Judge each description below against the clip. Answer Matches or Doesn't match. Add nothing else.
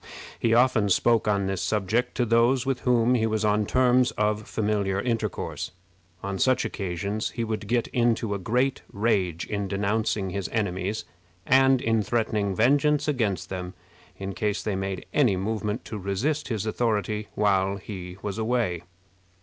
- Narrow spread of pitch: Doesn't match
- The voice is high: Doesn't match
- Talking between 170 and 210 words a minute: Doesn't match